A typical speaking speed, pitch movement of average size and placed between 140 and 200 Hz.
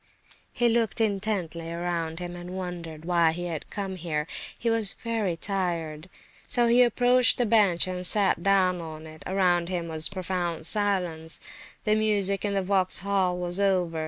Yes: average, 160 wpm; average, 3.1 semitones; medium, 185 Hz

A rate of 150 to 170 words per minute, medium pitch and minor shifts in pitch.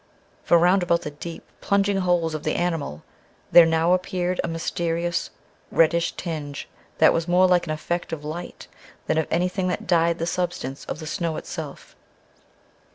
Yes: average, 165 wpm; medium, 170 Hz; narrow, 1.6 semitones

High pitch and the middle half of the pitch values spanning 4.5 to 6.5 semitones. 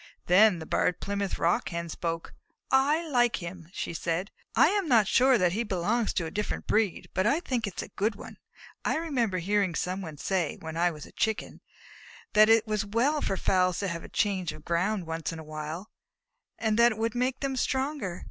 Yes: high, 200 Hz; average, 5.3 semitones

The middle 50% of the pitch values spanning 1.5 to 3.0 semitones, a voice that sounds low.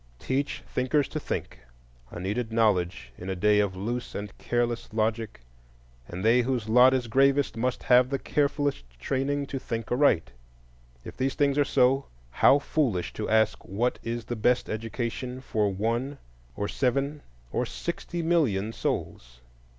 No: average, 4.5 semitones; low, 120 Hz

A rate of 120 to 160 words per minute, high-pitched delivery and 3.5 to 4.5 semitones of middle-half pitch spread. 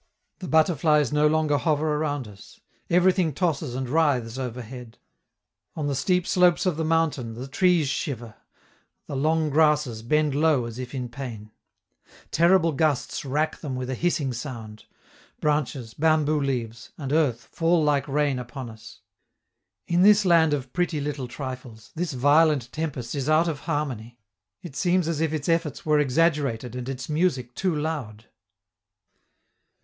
No: average, 155 wpm; medium, 145 Hz; average, 4.1 semitones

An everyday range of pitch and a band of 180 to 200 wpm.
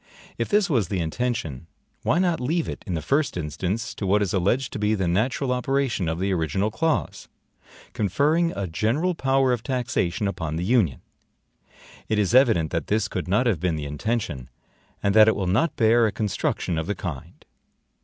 No: wide, 5.9 semitones; average, 190 wpm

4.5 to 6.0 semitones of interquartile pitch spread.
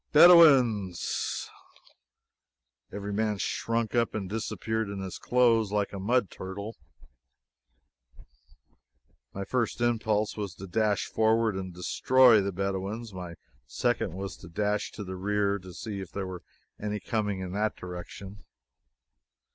No: average, 2.7 semitones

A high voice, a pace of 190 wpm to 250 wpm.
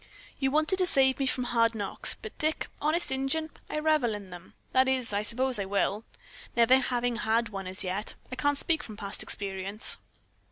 Yes: high, 245 Hz; average, 195 wpm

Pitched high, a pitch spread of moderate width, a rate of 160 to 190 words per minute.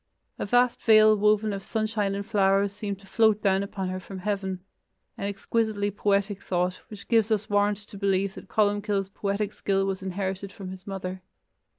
No: high, 200 Hz; narrow, 1.5 semitones; average, 180 wpm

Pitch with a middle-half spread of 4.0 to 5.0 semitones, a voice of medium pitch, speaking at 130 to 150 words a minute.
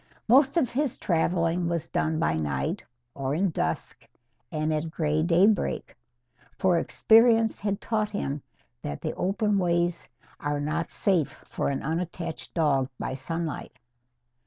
Yes: average, 4.7 semitones; medium, 170 Hz; slow, 135 wpm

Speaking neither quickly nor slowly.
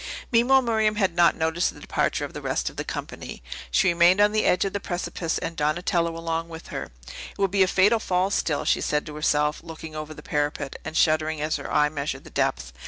No: fast, 230 wpm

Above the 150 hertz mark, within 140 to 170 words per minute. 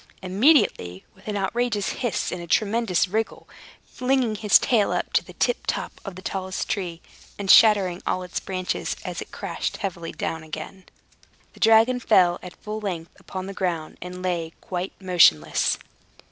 Yes: high, 190 Hz; average, 165 wpm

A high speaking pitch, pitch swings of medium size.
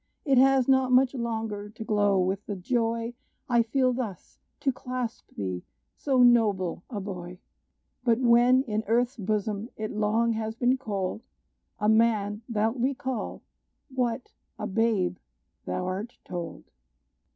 Yes: high, 225 Hz; average, 3.3 semitones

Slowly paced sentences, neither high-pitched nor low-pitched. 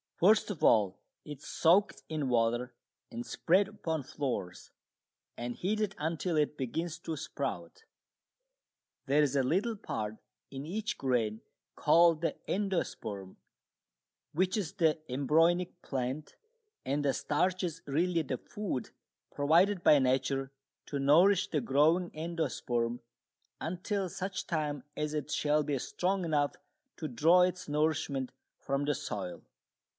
Yes: slow, 130 wpm; medium, 150 Hz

